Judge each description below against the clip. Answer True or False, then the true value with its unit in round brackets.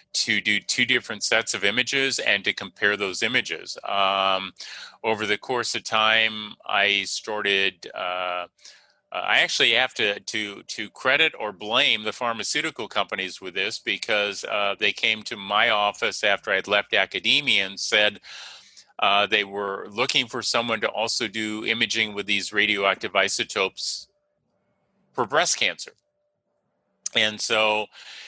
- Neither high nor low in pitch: False (105 Hz)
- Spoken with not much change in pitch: True (2.0 semitones)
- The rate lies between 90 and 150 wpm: True (140 wpm)